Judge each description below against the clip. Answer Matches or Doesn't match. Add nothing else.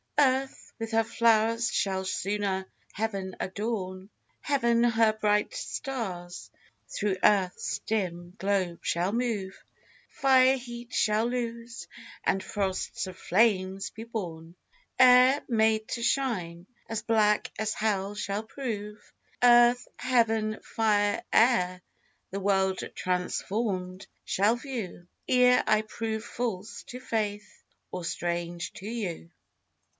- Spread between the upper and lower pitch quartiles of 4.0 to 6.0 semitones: Doesn't match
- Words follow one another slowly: Matches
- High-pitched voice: Matches